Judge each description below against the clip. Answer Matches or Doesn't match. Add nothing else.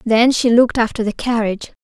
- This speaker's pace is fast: Doesn't match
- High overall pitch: Matches